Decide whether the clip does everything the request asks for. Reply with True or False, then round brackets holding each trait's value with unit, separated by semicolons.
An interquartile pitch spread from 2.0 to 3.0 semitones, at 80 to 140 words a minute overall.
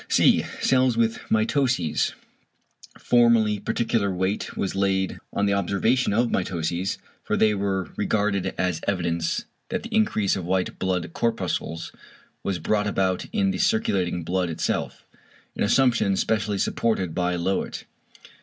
False (3.7 semitones; 135 wpm)